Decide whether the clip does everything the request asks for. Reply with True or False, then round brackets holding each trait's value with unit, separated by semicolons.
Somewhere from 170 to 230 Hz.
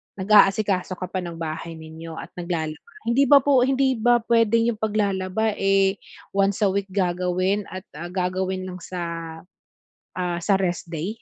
True (190 Hz)